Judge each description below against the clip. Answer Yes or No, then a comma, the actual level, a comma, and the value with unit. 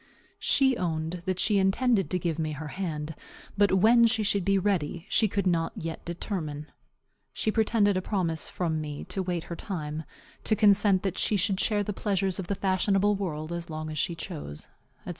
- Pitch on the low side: No, medium, 185 Hz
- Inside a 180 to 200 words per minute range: Yes, average, 195 wpm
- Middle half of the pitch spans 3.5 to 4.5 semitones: Yes, average, 3.9 semitones